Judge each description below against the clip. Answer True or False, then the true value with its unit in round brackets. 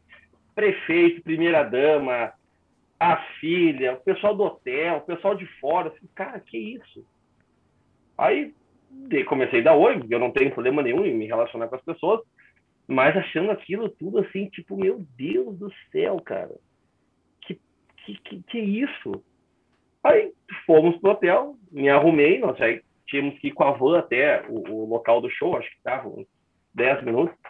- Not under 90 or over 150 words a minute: False (170 wpm)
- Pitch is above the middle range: True (195 Hz)